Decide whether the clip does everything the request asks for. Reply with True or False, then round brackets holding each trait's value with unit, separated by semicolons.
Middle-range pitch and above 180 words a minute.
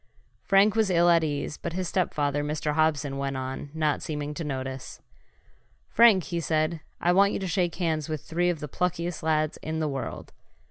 True (160 Hz; 190 wpm)